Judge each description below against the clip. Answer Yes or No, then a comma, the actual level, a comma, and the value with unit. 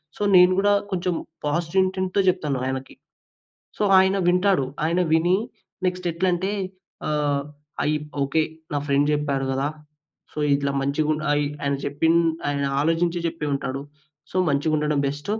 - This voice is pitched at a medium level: Yes, medium, 155 Hz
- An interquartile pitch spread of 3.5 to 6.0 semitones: Yes, average, 4.2 semitones